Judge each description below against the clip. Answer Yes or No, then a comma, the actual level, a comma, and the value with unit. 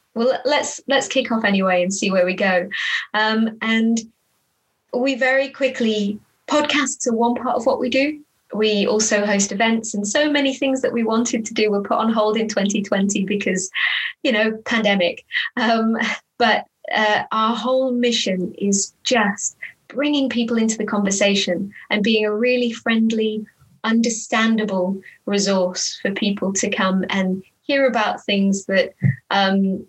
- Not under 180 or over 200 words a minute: No, average, 155 wpm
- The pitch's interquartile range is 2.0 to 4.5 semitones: Yes, average, 3.7 semitones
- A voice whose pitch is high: Yes, high, 220 Hz